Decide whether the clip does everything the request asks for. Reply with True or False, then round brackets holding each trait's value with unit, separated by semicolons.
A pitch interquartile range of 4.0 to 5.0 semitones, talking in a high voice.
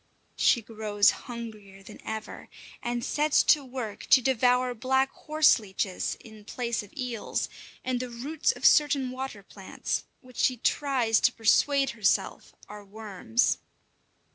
False (3.4 semitones; 240 Hz)